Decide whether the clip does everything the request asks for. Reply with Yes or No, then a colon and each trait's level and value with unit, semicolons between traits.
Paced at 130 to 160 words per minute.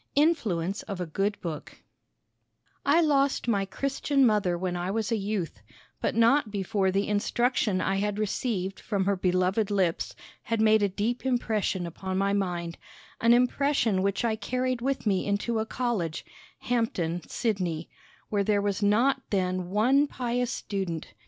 Yes: average, 155 wpm